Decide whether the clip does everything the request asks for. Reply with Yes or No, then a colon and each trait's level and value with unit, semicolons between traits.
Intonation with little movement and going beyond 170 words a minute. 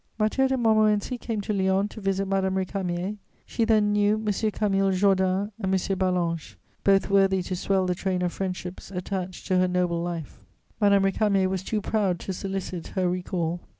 Yes: narrow, 2.0 semitones; average, 180 wpm